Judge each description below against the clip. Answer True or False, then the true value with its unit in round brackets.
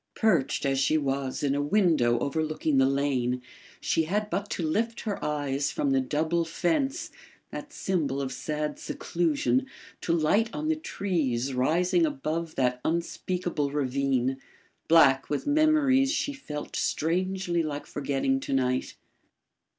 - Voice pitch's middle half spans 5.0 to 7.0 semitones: True (5.6 semitones)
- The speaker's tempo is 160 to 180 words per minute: False (140 wpm)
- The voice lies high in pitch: False (155 Hz)